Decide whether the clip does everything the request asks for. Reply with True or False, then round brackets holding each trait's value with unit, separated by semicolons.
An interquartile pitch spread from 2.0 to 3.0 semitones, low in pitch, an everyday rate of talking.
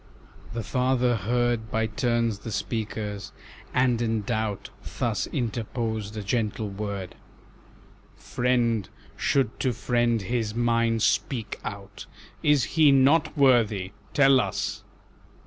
False (2.6 semitones; 115 Hz; 115 wpm)